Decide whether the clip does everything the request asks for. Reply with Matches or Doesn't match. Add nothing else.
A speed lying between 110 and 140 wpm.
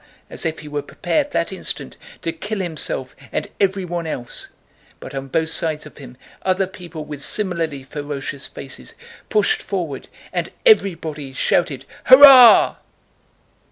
Matches